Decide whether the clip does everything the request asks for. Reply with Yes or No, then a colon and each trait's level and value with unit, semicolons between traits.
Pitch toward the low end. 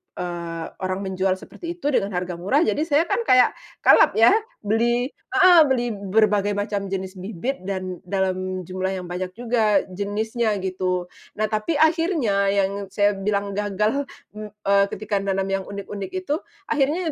No: high, 200 Hz